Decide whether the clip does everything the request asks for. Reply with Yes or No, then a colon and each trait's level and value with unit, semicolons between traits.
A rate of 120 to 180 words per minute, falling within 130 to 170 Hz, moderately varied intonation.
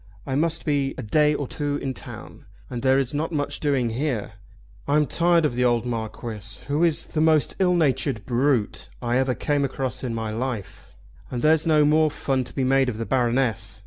No: average, 200 wpm; low, 135 Hz; average, 3.8 semitones